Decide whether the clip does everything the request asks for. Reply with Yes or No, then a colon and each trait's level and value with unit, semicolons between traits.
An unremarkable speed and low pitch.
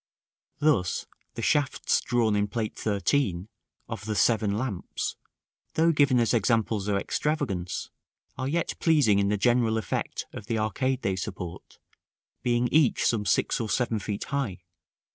Yes: average, 145 wpm; low, 110 Hz